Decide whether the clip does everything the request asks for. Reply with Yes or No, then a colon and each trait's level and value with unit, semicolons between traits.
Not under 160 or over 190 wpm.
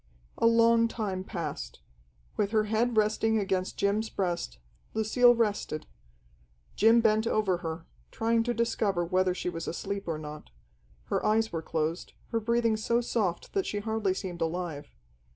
No: average, 150 wpm